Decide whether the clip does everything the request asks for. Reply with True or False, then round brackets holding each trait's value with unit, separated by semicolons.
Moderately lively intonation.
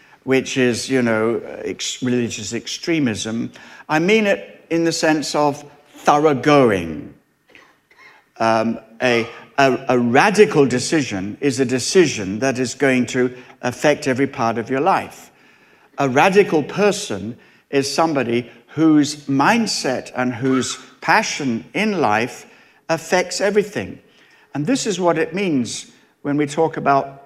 True (4.4 semitones)